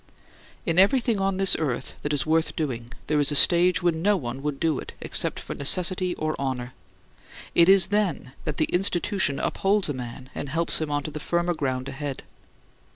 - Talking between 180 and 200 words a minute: Yes, average, 195 wpm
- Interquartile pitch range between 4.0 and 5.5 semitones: Yes, average, 4.7 semitones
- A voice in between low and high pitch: Yes, medium, 155 Hz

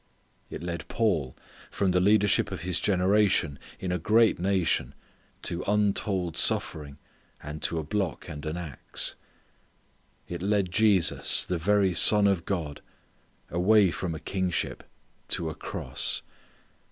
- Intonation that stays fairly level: No, average, 3.7 semitones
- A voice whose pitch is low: Yes, very low, 90 Hz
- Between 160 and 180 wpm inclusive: No, slow, 135 wpm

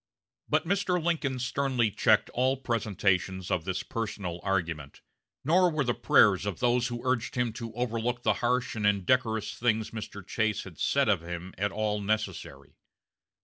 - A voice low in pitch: Yes, low, 110 Hz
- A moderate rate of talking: Yes, average, 160 wpm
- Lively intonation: No, average, 4.4 semitones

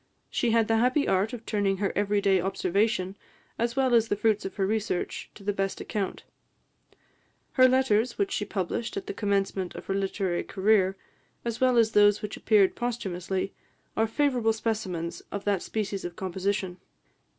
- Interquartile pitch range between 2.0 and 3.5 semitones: Yes, average, 2.8 semitones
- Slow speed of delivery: No, average, 175 wpm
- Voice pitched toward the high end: Yes, high, 205 Hz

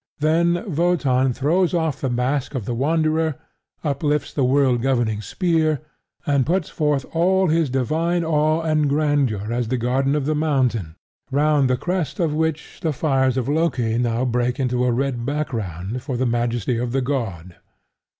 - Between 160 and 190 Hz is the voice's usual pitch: No, medium, 140 Hz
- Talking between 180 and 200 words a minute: No, average, 165 wpm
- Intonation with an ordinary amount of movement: Yes, average, 4.1 semitones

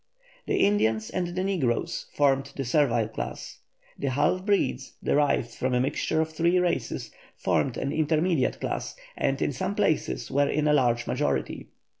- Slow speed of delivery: No, average, 160 wpm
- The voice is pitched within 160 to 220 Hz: No, medium, 145 Hz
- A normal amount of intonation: Yes, average, 4.7 semitones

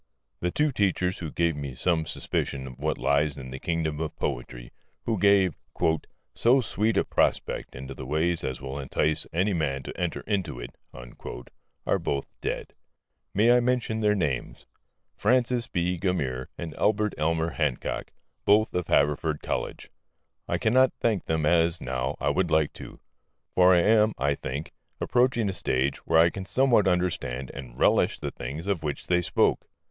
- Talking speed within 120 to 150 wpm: No, average, 170 wpm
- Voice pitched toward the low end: Yes, very low, 85 Hz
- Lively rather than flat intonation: Yes, wide, 6.2 semitones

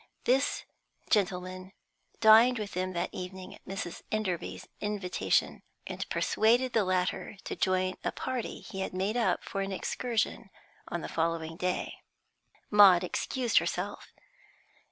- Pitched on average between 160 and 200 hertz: Yes, high, 190 Hz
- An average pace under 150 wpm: Yes, slow, 135 wpm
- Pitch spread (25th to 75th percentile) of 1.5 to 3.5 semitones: Yes, average, 3.0 semitones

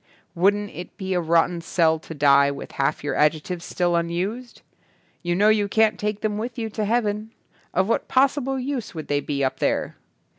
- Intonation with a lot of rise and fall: No, average, 4.7 semitones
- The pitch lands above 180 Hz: Yes, high, 190 Hz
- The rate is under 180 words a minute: No, average, 200 wpm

